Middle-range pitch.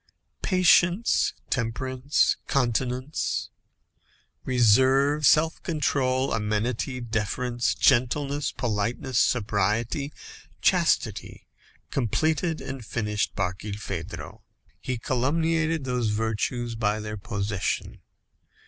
No: low, 125 Hz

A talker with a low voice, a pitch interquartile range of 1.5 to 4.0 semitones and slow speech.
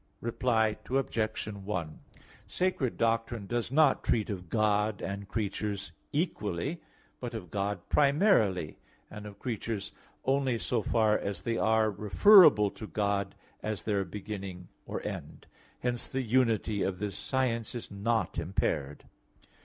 Yes: low, 110 Hz; average, 3.1 semitones; slow, 130 wpm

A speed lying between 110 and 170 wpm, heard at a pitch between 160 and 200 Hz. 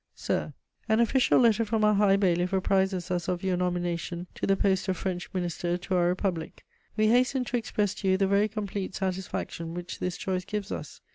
No: fast, 205 wpm; high, 190 Hz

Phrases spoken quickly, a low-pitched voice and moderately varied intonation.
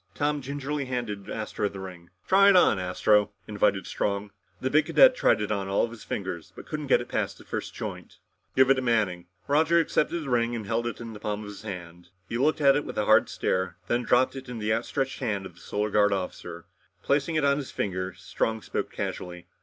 No: fast, 230 wpm; low, 110 Hz; wide, 5.7 semitones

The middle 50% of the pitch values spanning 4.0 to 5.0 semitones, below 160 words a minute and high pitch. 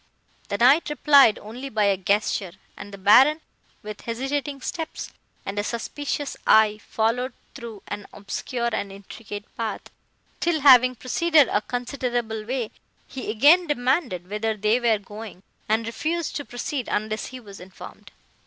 Yes: average, 4.4 semitones; average, 145 wpm; high, 230 Hz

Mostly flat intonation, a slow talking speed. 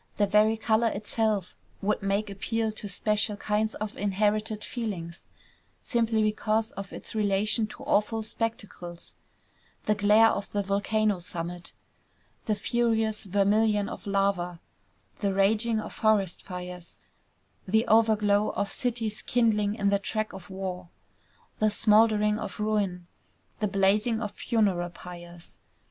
Yes: narrow, 1.9 semitones; slow, 130 wpm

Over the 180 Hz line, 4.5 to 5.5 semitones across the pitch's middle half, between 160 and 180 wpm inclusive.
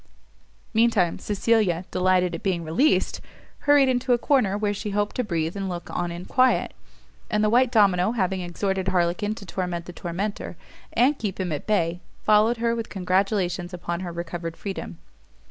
No: high, 190 Hz; average, 3.7 semitones; average, 175 wpm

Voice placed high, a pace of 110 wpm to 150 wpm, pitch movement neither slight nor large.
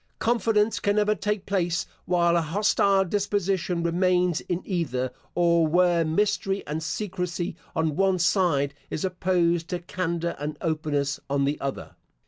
No: medium, 175 Hz; average, 140 wpm; average, 3.0 semitones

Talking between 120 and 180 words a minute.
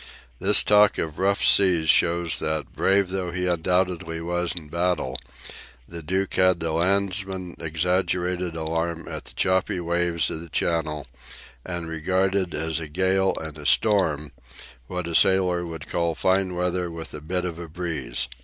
Yes: average, 160 wpm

